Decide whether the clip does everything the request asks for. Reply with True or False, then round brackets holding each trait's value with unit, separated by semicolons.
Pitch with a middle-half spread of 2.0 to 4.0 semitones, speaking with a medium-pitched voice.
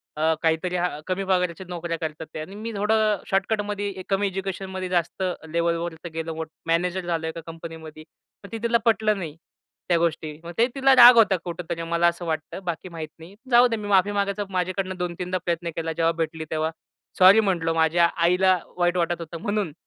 True (3.0 semitones; 180 Hz)